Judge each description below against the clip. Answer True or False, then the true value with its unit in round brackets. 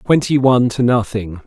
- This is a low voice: True (120 Hz)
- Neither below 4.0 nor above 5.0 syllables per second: False (5.3 syllables/s)